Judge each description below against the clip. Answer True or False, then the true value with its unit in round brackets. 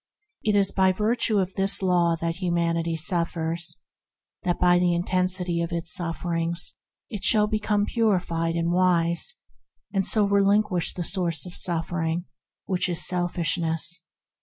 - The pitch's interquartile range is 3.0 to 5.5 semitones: False (2.4 semitones)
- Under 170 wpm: True (155 wpm)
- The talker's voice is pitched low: False (175 Hz)